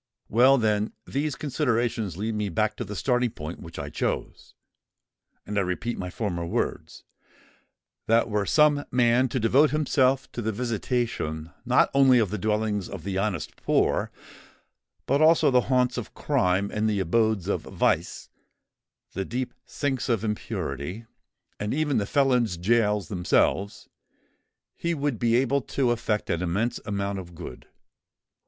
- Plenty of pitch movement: No, average, 4.4 semitones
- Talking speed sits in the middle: Yes, average, 150 wpm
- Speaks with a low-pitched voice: Yes, low, 110 Hz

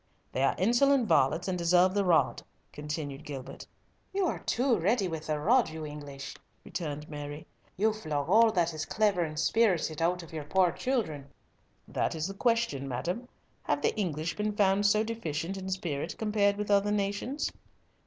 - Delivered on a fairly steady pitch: No, wide, 5.5 semitones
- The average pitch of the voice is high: No, medium, 180 Hz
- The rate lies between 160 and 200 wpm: Yes, average, 175 wpm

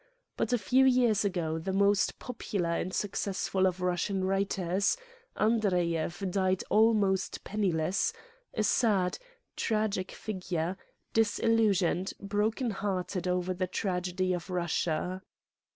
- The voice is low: No, high, 190 Hz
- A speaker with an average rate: No, slow, 120 wpm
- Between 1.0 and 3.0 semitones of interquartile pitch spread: Yes, average, 2.7 semitones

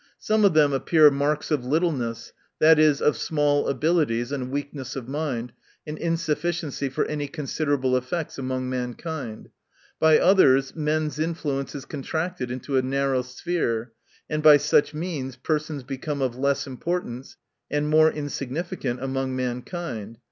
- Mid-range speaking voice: Yes, medium, 145 Hz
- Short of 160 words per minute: Yes, average, 150 wpm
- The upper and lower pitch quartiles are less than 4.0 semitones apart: Yes, average, 3.2 semitones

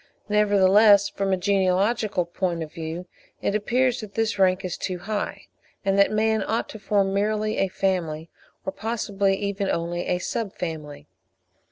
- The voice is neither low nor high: No, high, 195 Hz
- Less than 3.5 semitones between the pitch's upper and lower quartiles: Yes, narrow, 2.6 semitones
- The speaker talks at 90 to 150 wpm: No, average, 160 wpm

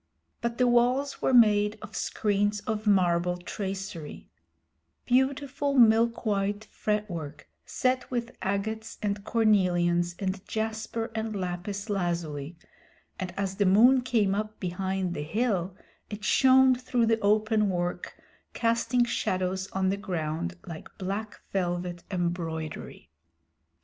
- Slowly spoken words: Yes, slow, 120 wpm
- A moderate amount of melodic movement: Yes, average, 3.9 semitones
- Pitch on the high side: Yes, high, 205 Hz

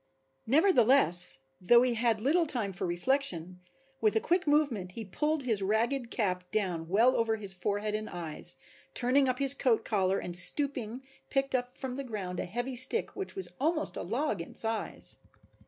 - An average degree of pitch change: No, wide, 5.8 semitones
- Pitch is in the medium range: No, high, 230 Hz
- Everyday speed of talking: Yes, average, 175 wpm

